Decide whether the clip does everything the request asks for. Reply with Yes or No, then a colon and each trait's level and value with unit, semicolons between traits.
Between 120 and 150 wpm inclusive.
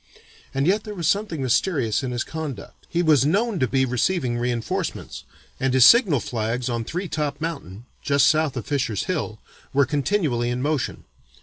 No: average, 175 wpm